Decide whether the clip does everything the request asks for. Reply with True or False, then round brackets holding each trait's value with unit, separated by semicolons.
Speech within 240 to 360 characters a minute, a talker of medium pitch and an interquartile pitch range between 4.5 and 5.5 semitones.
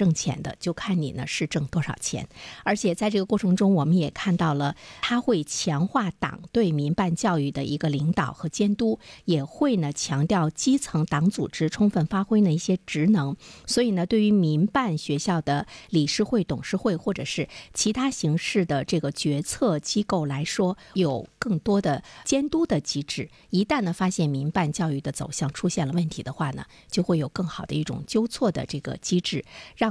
True (280 characters per minute; 175 Hz; 5.1 semitones)